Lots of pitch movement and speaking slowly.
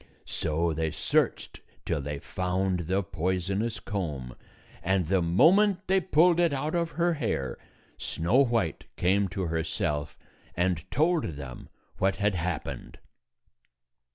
Yes: wide, 8.8 semitones; slow, 125 wpm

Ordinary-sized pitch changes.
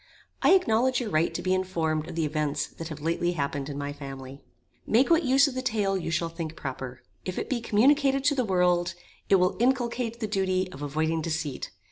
No: wide, 7.3 semitones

